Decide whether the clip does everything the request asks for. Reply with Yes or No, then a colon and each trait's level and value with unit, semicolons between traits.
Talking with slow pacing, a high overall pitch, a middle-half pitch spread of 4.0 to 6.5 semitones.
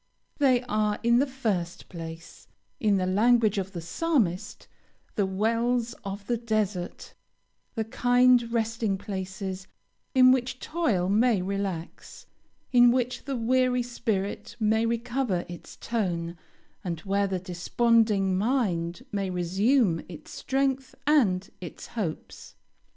Yes: slow, 125 wpm; high, 215 Hz; average, 4.6 semitones